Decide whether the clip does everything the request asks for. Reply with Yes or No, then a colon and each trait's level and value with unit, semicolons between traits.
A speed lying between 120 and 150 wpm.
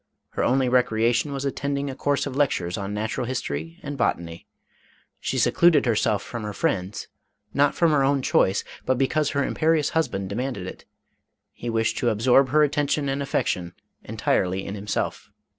No: average, 170 wpm